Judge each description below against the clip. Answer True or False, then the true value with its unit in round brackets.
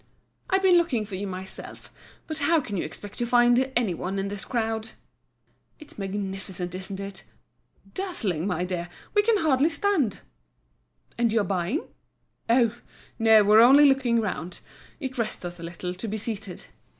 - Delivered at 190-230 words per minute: False (160 wpm)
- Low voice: False (220 Hz)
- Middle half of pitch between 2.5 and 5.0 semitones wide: False (5.5 semitones)